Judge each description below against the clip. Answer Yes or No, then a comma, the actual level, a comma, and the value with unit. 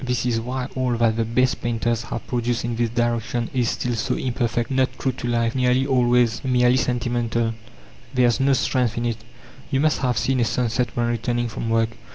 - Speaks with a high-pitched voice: No, low, 120 Hz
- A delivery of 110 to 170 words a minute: No, fast, 205 wpm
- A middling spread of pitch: No, narrow, 1.3 semitones